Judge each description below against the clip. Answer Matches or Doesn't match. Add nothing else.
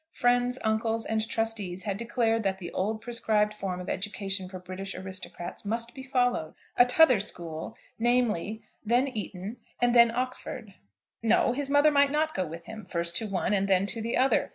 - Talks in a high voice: Matches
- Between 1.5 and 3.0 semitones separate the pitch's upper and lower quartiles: Doesn't match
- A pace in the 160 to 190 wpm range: Matches